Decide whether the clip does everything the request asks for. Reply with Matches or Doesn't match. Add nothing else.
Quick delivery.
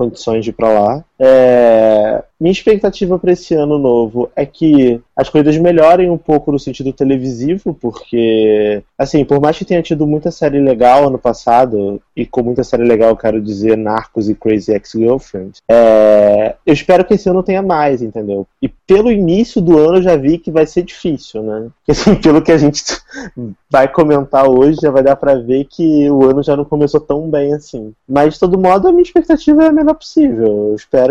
Matches